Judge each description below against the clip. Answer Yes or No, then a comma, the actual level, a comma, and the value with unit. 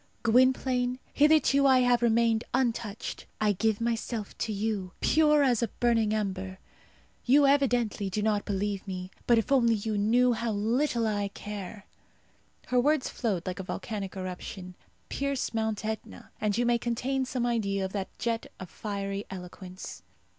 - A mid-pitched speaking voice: No, high, 225 Hz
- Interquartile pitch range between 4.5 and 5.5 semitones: No, average, 3.5 semitones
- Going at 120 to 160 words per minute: Yes, average, 155 wpm